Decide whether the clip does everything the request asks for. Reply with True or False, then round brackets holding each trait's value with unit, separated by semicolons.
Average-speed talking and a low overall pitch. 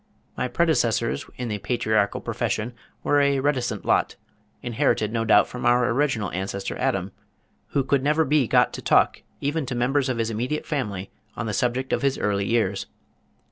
True (175 wpm; 120 Hz)